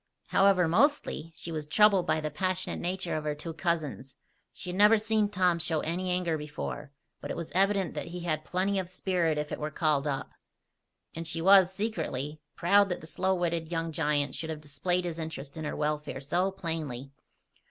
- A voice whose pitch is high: No, medium, 165 Hz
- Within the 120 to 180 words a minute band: No, average, 195 wpm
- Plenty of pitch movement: No, average, 3.4 semitones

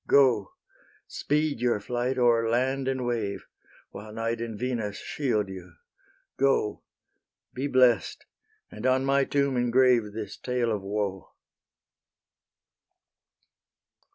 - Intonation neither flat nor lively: Yes, average, 3.5 semitones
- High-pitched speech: No, low, 120 Hz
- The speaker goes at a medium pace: No, slow, 110 wpm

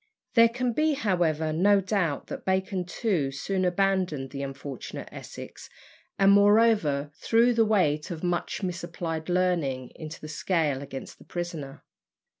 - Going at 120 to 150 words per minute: Yes, average, 140 wpm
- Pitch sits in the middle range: Yes, medium, 175 Hz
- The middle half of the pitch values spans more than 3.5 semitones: Yes, average, 4.9 semitones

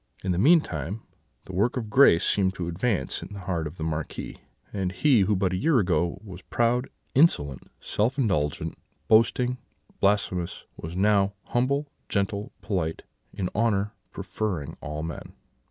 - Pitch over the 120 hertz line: No, low, 100 Hz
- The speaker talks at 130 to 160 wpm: Yes, average, 155 wpm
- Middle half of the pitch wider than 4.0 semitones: Yes, average, 4.8 semitones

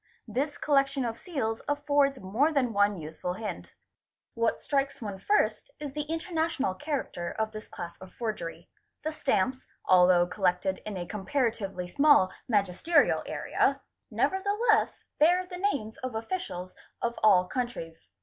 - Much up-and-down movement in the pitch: Yes, wide, 7.5 semitones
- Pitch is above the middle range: Yes, high, 235 Hz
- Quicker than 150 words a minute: No, average, 145 wpm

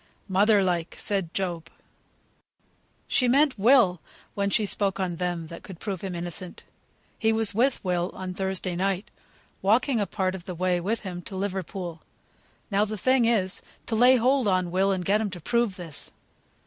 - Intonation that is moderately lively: Yes, average, 3.3 semitones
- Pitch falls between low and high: No, high, 195 Hz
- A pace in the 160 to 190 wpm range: Yes, average, 175 wpm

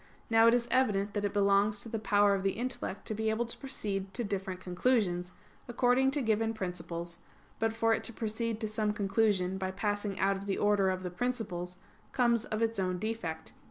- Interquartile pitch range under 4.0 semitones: Yes, average, 2.9 semitones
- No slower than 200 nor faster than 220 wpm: Yes, fast, 205 wpm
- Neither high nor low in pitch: No, high, 210 Hz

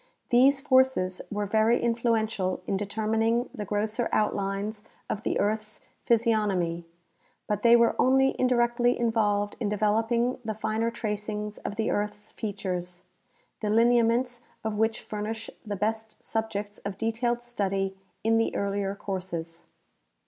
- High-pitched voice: Yes, high, 215 Hz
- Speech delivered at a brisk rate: No, slow, 135 wpm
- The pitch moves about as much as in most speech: No, narrow, 2.3 semitones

